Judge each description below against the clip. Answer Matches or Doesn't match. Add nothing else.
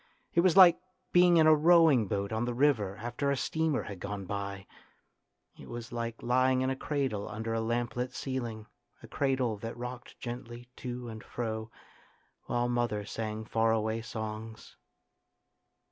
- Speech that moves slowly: Doesn't match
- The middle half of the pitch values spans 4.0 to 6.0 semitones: Doesn't match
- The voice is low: Matches